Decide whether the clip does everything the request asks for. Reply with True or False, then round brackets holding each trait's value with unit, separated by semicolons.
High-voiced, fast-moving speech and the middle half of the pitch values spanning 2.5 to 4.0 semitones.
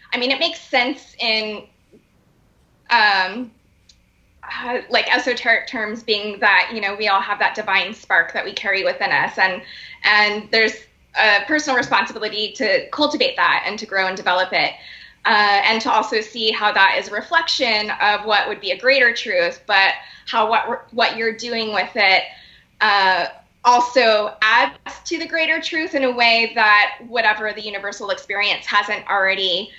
False (215 Hz; 165 wpm; 3.5 semitones)